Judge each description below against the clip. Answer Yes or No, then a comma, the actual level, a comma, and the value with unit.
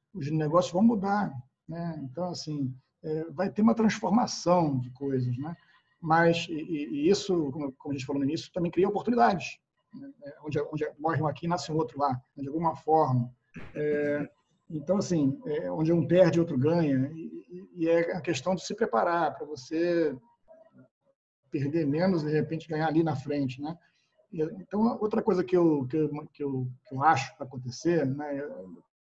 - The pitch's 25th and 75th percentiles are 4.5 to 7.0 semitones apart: No, average, 3.8 semitones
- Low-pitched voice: No, medium, 160 Hz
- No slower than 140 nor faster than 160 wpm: No, average, 180 wpm